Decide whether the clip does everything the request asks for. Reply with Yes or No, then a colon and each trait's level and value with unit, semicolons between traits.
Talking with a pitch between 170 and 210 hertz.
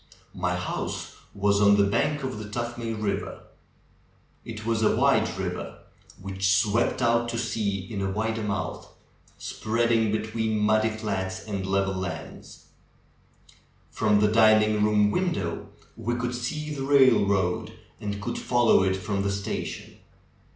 No: low, 105 Hz